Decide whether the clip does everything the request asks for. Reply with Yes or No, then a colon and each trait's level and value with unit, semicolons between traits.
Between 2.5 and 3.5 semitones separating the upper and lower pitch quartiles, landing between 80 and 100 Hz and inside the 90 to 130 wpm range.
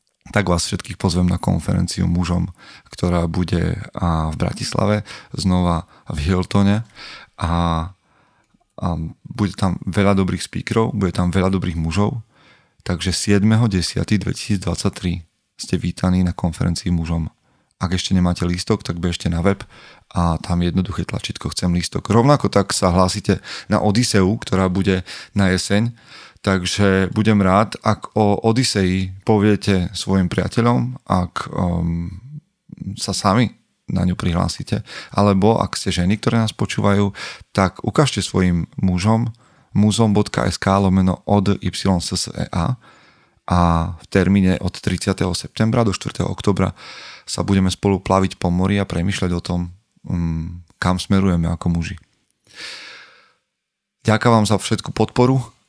Yes: average, 2.9 semitones; very low, 95 Hz; average, 125 wpm